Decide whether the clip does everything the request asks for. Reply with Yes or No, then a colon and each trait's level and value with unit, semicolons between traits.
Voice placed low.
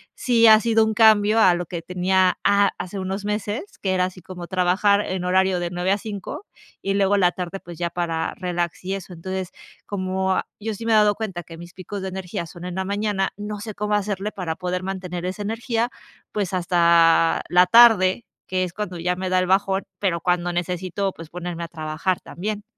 No: medium, 185 Hz